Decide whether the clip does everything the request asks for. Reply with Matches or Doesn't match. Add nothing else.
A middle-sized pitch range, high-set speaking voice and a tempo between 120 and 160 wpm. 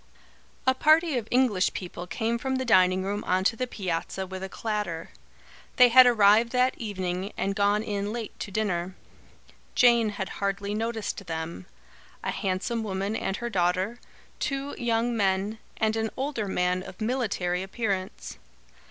Matches